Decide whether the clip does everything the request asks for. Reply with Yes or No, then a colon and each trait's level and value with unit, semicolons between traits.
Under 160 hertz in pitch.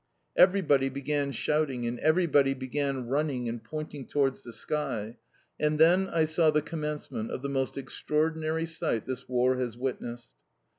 Yes: medium, 140 Hz